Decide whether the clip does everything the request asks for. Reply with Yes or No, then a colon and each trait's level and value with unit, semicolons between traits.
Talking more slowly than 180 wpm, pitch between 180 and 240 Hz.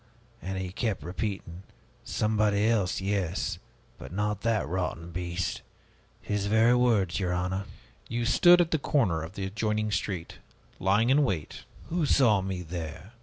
No: average, 150 wpm; low, 100 Hz